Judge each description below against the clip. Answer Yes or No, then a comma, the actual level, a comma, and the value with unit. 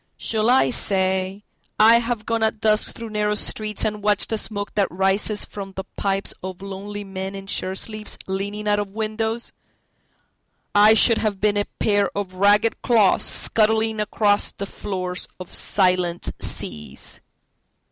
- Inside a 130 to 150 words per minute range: Yes, average, 140 wpm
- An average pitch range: No, narrow, 2.0 semitones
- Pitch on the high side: Yes, high, 205 Hz